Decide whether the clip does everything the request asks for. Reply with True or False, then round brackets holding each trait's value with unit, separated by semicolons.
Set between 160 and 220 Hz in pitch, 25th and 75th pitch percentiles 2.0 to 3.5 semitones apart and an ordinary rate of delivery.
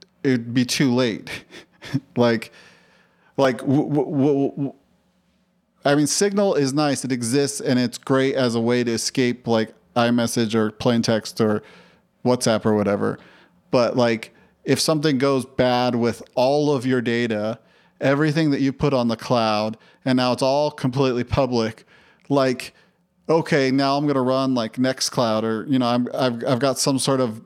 False (130 Hz; 2.9 semitones; 170 wpm)